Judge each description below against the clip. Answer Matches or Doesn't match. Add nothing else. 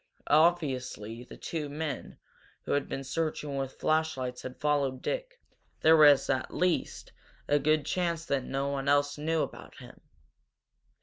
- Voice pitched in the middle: Matches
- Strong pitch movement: Doesn't match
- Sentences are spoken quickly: Doesn't match